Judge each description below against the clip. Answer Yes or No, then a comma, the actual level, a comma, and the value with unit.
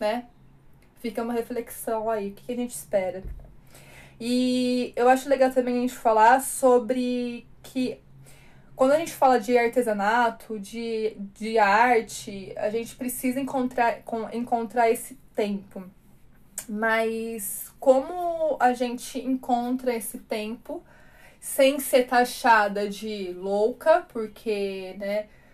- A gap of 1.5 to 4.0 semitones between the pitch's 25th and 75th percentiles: Yes, narrow, 2.6 semitones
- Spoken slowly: Yes, slow, 115 wpm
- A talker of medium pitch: No, high, 235 Hz